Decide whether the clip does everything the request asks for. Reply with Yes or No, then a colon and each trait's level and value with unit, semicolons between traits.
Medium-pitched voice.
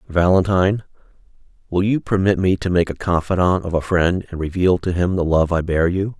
No: very low, 90 Hz